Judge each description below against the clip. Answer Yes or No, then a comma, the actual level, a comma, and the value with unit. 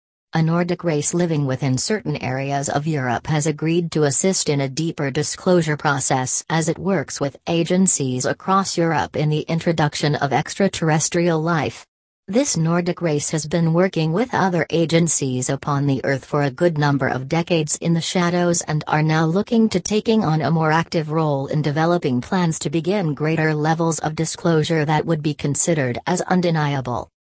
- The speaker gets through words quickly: No, average, 170 wpm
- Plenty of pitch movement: No, average, 3.0 semitones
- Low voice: No, medium, 160 Hz